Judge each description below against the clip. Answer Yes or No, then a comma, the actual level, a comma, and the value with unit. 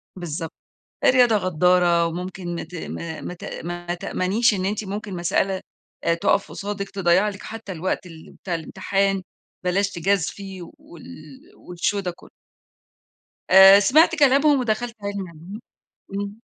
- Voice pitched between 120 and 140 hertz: No, high, 190 Hz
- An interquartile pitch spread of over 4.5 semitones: No, average, 2.7 semitones